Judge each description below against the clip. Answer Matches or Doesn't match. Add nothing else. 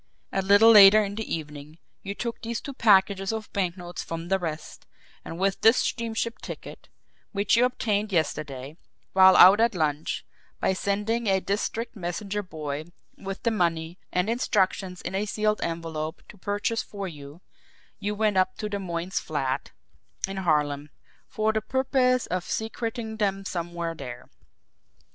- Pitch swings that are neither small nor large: Matches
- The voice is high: Matches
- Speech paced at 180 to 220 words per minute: Doesn't match